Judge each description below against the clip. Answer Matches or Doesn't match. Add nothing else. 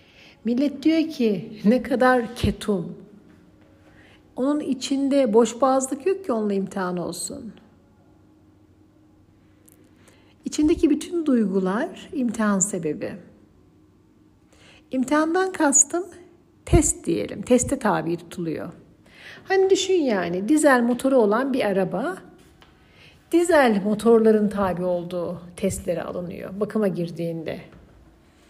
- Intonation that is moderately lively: Doesn't match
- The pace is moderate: Doesn't match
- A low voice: Doesn't match